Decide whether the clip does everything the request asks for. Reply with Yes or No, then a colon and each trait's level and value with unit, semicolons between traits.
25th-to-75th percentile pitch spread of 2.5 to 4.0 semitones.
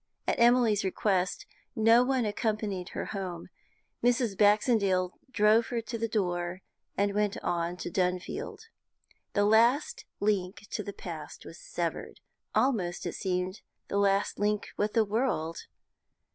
Yes: average, 3.6 semitones